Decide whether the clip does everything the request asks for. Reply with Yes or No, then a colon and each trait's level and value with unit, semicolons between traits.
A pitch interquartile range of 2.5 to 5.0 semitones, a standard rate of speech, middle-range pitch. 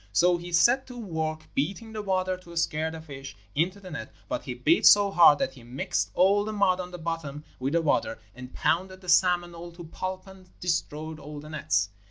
No: average, 3.6 semitones; fast, 220 wpm; medium, 170 Hz